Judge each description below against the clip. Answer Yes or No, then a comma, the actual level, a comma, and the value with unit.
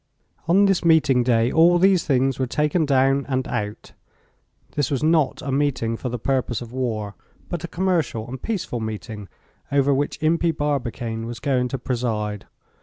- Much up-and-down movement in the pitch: No, average, 4.6 semitones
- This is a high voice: No, low, 135 Hz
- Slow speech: No, average, 170 wpm